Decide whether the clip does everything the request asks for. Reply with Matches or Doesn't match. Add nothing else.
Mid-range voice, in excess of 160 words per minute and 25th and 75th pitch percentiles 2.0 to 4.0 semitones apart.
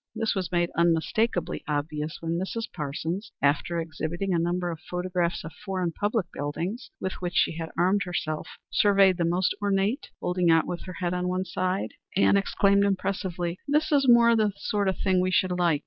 Matches